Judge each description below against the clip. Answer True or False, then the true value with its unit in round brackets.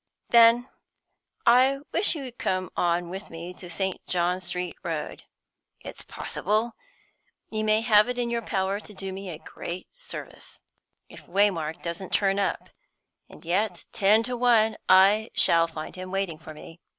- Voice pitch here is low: False (195 Hz)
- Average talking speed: True (160 wpm)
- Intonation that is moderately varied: True (4.1 semitones)